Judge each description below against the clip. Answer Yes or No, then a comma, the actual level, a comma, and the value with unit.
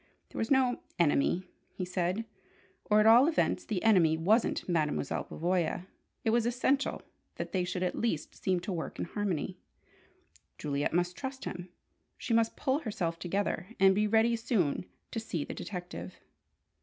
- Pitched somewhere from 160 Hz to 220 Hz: Yes, high, 190 Hz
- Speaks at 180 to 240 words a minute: No, average, 160 wpm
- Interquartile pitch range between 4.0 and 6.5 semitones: Yes, average, 4.5 semitones